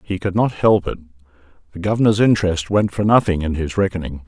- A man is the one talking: Yes, male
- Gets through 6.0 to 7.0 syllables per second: Yes, 6.2 syllables/s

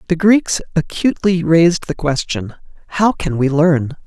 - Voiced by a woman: No, male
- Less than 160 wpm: Yes, average, 150 wpm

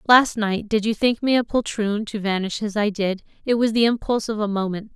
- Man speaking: No, female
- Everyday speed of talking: No, fast, 240 wpm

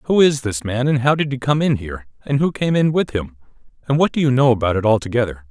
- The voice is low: Yes, low, 125 Hz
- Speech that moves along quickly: Yes, fast, 270 wpm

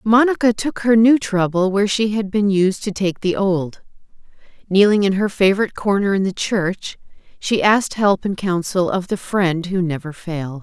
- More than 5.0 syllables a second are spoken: No, 4.8 syllables/s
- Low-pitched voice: No, high, 195 Hz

